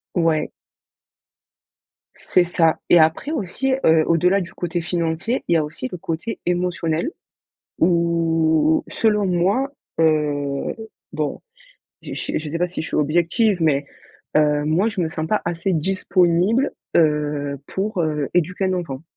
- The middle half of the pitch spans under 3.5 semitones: Yes, average, 2.8 semitones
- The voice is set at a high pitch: No, medium, 170 Hz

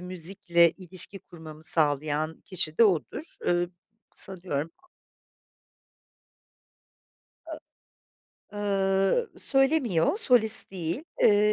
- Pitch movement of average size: Yes, average, 4.2 semitones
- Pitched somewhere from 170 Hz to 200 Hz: Yes, medium, 185 Hz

